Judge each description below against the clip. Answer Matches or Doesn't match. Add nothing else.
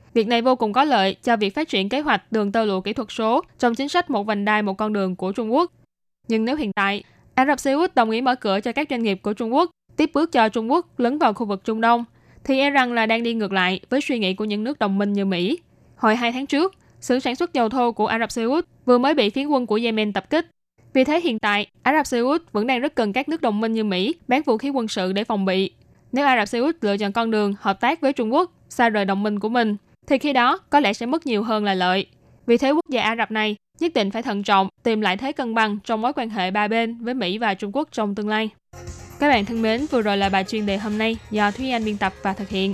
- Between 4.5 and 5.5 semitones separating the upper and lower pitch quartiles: Doesn't match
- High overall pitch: Matches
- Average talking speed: Doesn't match